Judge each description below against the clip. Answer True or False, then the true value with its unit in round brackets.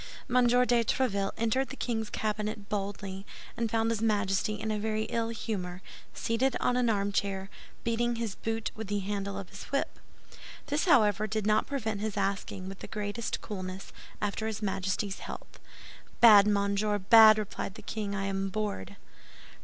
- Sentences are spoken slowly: False (165 wpm)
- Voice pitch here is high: True (210 Hz)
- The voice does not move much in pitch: True (2.3 semitones)